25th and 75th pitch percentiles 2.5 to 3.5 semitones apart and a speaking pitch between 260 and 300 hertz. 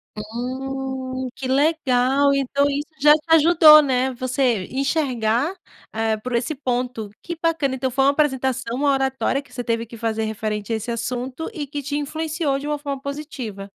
Yes: average, 3.0 semitones; very high, 265 Hz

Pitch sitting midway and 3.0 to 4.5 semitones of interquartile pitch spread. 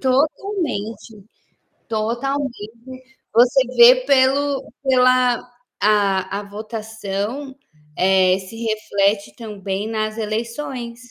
No: high, 230 Hz; average, 3.8 semitones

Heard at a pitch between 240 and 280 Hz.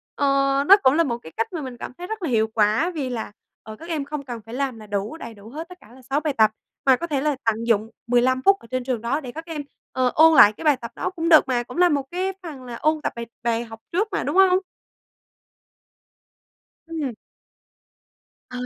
Yes: very high, 270 Hz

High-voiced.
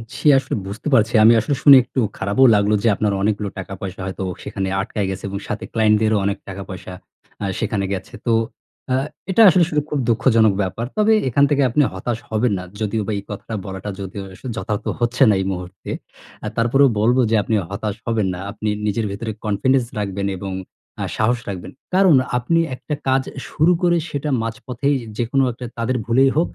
No: low, 110 Hz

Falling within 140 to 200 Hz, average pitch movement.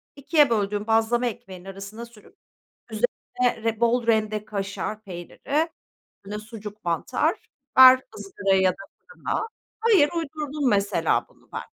No: high, 225 Hz; average, 4.1 semitones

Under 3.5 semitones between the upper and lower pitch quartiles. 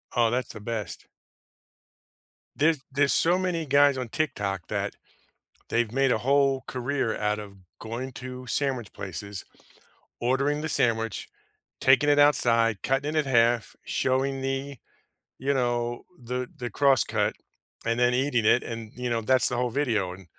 Yes: average, 3.1 semitones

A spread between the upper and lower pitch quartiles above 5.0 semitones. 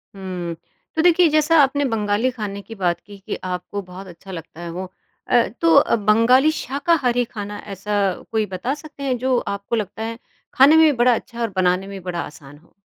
Yes: wide, 5.6 semitones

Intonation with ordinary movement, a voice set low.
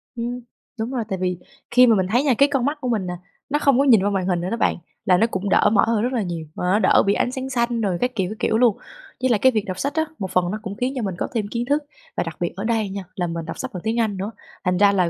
No: average, 4.6 semitones; high, 215 Hz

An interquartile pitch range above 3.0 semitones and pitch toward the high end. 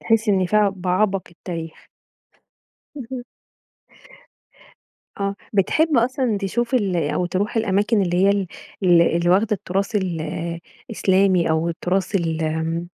Yes: average, 3.4 semitones; high, 195 Hz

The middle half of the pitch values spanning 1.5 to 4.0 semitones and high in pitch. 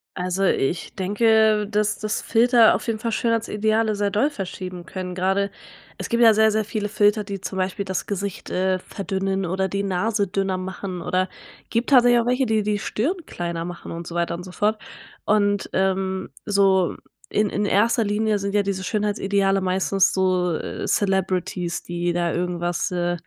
Yes: narrow, 2.6 semitones; high, 195 Hz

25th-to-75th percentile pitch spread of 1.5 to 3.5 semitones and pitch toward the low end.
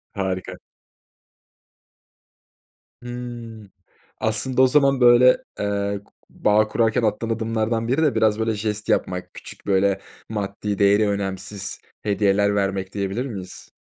Yes: narrow, 2.4 semitones; low, 105 Hz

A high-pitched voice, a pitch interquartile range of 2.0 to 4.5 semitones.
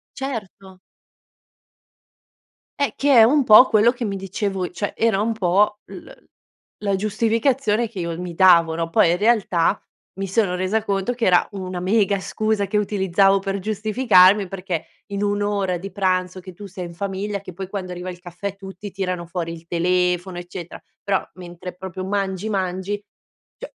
Yes: high, 195 Hz; narrow, 2.4 semitones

